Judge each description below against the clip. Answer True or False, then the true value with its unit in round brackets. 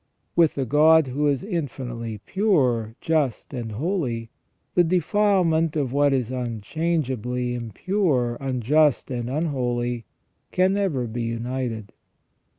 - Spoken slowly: True (115 wpm)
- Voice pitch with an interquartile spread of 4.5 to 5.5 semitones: True (5.1 semitones)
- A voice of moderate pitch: False (130 Hz)